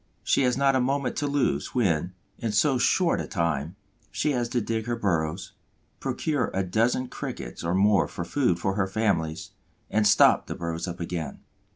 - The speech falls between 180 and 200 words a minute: Yes, average, 185 wpm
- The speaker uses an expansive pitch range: Yes, wide, 6.6 semitones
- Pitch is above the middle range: No, low, 105 Hz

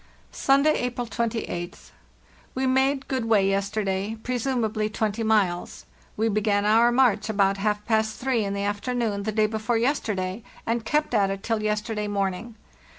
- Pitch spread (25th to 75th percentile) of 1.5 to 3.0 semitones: Yes, average, 2.7 semitones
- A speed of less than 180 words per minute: Yes, average, 155 wpm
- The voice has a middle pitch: No, high, 220 Hz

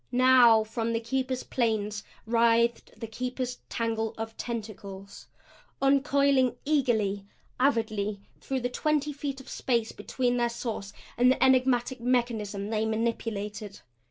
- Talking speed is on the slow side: Yes, slow, 125 wpm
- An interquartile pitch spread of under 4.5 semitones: Yes, average, 2.8 semitones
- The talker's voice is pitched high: Yes, high, 235 Hz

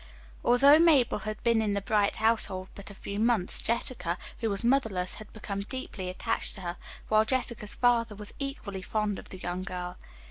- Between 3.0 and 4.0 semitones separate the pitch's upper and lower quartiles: Yes, average, 3.5 semitones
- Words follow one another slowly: No, average, 185 wpm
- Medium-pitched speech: No, high, 215 Hz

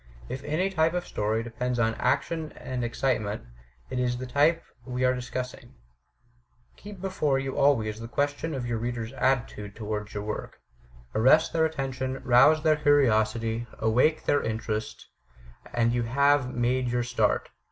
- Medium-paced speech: Yes, average, 155 wpm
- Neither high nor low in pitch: No, low, 125 Hz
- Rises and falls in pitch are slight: No, average, 3.8 semitones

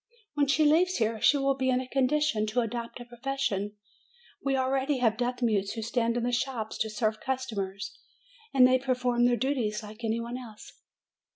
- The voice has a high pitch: Yes, high, 245 Hz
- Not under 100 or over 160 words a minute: No, average, 190 wpm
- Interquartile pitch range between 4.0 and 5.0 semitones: No, average, 3.2 semitones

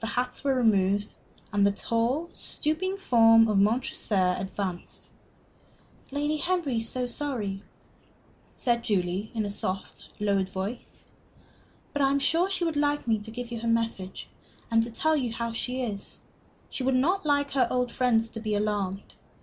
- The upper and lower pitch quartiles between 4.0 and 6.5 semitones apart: Yes, average, 5.0 semitones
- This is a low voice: No, high, 230 Hz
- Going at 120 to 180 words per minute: Yes, average, 165 wpm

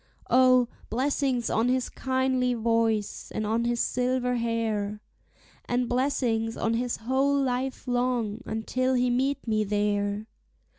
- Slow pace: Yes, slow, 130 wpm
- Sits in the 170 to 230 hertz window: No, high, 245 Hz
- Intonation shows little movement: Yes, narrow, 2.3 semitones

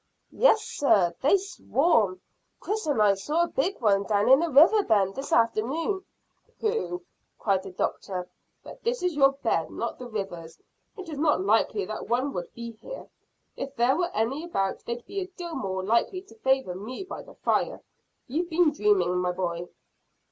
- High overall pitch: Yes, very high, 255 Hz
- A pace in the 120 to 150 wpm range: No, average, 180 wpm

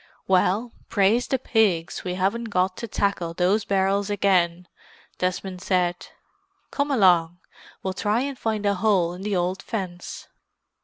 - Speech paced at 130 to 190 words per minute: Yes, average, 140 wpm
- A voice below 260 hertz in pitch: Yes, high, 190 Hz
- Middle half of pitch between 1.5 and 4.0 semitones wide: Yes, average, 2.7 semitones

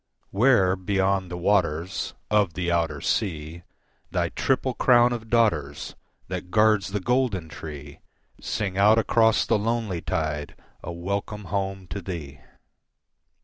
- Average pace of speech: No, slow, 130 wpm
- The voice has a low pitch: Yes, very low, 95 Hz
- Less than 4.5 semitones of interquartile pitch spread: Yes, average, 4.1 semitones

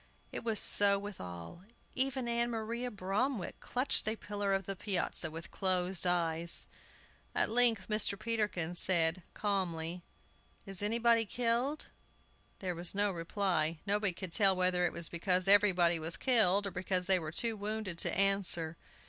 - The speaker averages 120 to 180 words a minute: Yes, average, 155 wpm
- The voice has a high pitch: Yes, high, 195 Hz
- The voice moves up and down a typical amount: Yes, average, 3.6 semitones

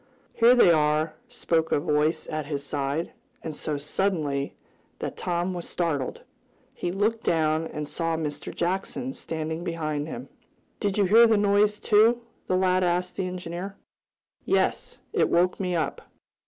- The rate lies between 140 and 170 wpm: Yes, average, 155 wpm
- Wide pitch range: No, average, 3.9 semitones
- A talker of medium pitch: Yes, medium, 170 Hz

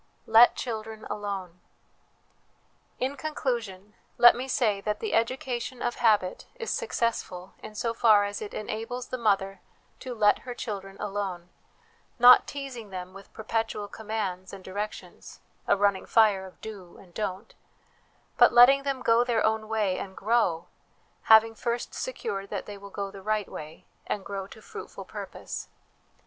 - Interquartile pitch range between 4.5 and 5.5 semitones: No, average, 3.2 semitones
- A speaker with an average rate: Yes, average, 155 wpm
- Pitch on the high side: Yes, high, 215 Hz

